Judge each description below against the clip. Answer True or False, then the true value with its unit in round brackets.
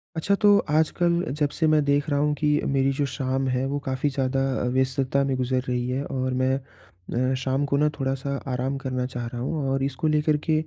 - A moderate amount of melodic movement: False (2.3 semitones)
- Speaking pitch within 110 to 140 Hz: True (135 Hz)